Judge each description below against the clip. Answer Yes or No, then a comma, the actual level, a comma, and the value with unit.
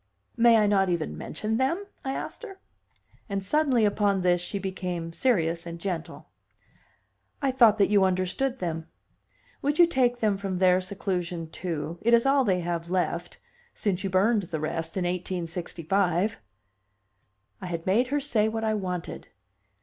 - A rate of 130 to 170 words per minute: Yes, average, 160 wpm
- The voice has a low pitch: No, high, 190 Hz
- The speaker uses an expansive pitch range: No, average, 4.3 semitones